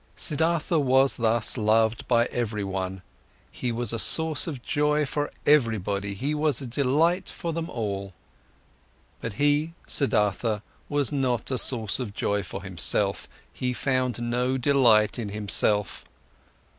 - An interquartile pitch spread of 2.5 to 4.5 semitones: No, average, 5.3 semitones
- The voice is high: No, low, 125 Hz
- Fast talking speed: No, slow, 135 wpm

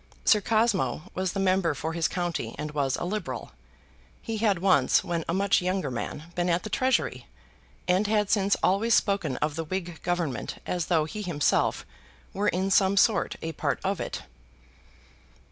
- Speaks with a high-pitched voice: No, medium, 180 Hz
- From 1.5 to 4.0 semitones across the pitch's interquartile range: Yes, average, 3.7 semitones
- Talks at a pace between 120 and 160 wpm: No, average, 175 wpm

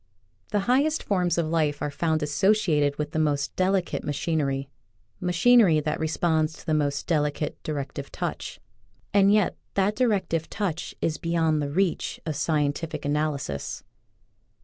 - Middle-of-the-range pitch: Yes, medium, 160 Hz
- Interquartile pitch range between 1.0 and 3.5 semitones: No, average, 4.0 semitones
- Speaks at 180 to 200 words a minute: No, average, 150 wpm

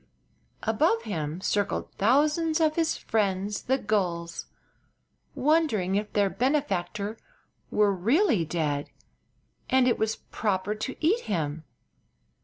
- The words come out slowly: Yes, slow, 110 wpm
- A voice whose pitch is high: Yes, high, 210 Hz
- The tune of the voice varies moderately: No, wide, 6.0 semitones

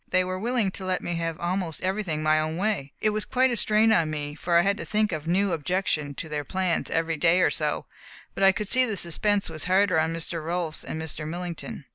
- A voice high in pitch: No, medium, 175 Hz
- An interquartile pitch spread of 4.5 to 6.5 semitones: No, average, 3.7 semitones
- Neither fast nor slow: No, fast, 245 wpm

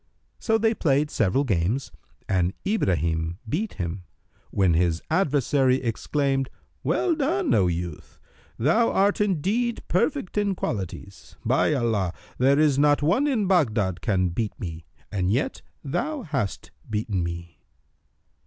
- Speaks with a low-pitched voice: Yes, low, 130 Hz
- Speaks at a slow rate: Yes, slow, 130 wpm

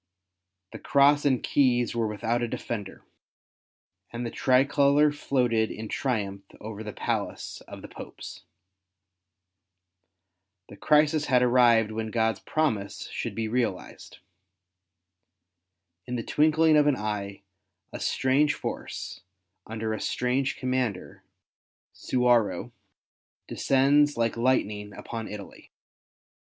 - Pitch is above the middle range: No, low, 120 Hz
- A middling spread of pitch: Yes, average, 4.0 semitones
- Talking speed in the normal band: No, slow, 110 wpm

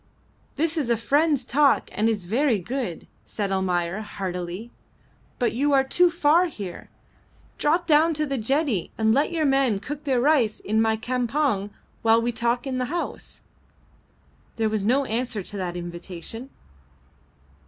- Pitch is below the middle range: No, high, 240 Hz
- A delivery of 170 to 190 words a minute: No, average, 155 wpm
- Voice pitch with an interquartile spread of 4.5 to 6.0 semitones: Yes, wide, 5.6 semitones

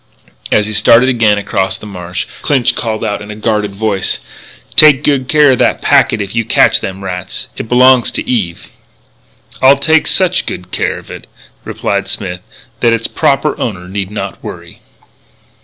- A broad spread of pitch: No, average, 4.5 semitones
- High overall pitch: No, low, 105 Hz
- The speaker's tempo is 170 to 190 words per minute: Yes, average, 175 wpm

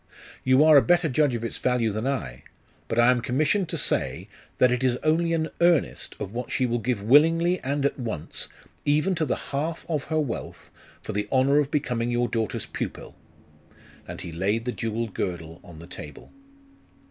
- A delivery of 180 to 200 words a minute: Yes, average, 195 wpm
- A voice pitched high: No, low, 125 Hz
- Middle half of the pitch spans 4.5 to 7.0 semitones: Yes, average, 5.0 semitones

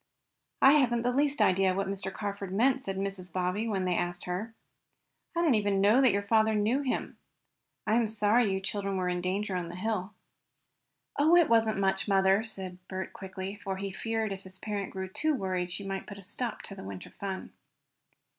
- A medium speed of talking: No, fast, 210 wpm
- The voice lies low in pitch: No, high, 200 Hz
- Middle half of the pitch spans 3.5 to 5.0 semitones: No, average, 2.8 semitones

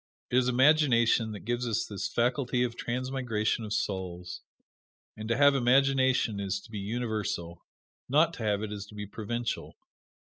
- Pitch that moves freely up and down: No, average, 3.3 semitones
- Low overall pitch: Yes, low, 115 Hz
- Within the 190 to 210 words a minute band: No, average, 165 wpm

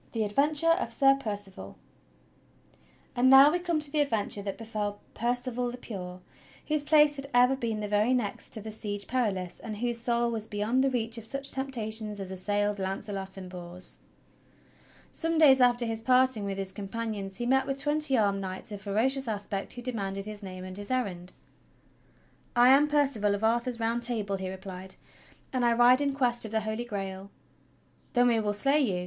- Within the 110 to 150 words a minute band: No, average, 190 wpm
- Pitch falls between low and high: No, high, 225 Hz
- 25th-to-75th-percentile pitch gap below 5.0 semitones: Yes, average, 4.2 semitones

